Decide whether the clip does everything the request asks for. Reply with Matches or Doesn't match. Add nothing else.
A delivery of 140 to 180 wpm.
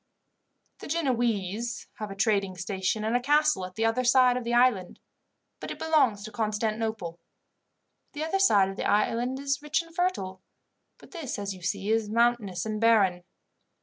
Matches